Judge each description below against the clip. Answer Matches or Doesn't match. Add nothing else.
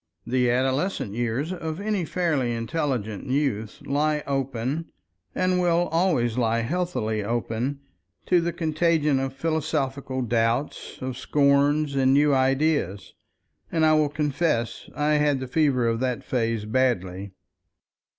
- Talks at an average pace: Doesn't match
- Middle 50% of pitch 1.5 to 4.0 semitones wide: Doesn't match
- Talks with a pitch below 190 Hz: Matches